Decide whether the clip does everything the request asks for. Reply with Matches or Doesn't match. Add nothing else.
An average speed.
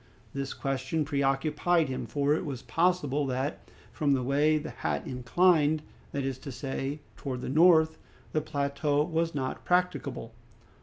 Matches